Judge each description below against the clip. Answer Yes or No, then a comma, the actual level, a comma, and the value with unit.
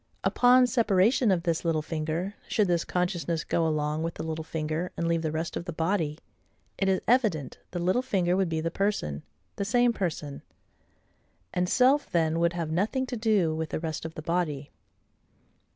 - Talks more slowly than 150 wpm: No, average, 185 wpm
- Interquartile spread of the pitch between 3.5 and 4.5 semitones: Yes, average, 3.9 semitones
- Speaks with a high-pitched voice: No, medium, 170 Hz